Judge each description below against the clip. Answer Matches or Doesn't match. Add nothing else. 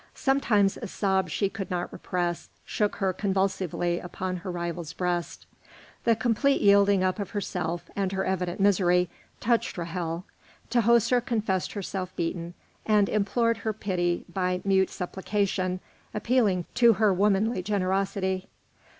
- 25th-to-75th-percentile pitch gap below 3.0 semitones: Matches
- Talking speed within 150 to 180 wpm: Doesn't match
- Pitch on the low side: Doesn't match